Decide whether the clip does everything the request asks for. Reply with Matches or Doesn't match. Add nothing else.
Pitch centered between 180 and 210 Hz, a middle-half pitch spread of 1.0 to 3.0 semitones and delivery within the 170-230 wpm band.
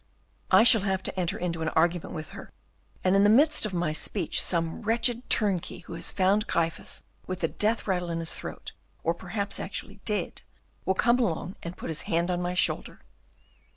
Doesn't match